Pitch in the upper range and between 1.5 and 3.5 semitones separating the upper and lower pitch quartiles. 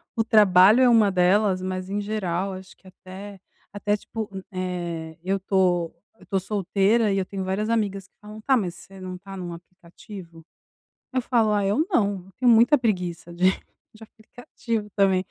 Yes: high, 195 Hz; narrow, 2.6 semitones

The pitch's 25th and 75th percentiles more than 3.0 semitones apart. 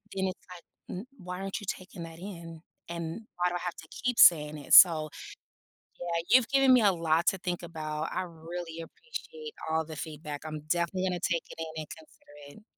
No: average, 2.7 semitones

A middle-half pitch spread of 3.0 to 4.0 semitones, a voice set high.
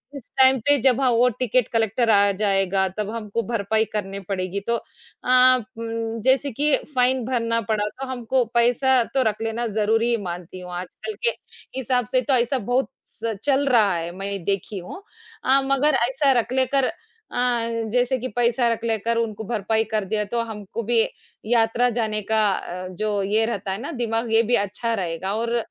Yes: average, 3.3 semitones; high, 230 Hz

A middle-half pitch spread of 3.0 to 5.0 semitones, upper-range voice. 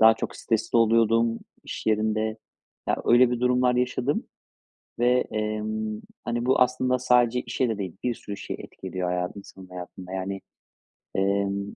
No: average, 3.6 semitones; low, 110 Hz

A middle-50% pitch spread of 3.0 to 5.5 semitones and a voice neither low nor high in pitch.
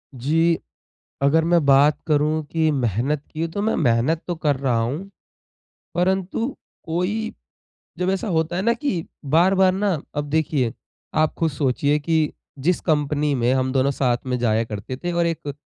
Yes: average, 4.3 semitones; medium, 155 Hz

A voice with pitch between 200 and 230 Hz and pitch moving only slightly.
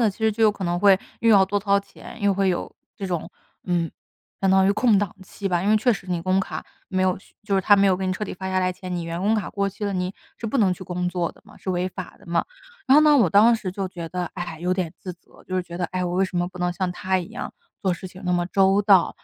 No: medium, 185 Hz; narrow, 2.0 semitones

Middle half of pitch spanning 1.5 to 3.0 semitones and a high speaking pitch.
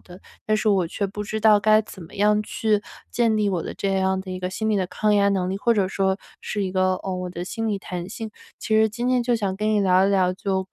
Yes: narrow, 2.4 semitones; high, 200 Hz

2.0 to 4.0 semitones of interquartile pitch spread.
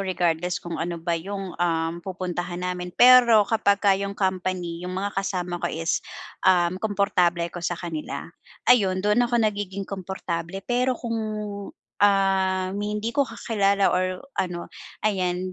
Yes: narrow, 2.4 semitones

